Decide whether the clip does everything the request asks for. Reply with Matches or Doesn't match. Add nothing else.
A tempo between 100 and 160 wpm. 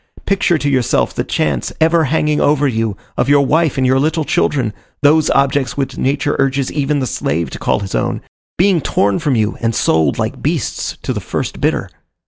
Doesn't match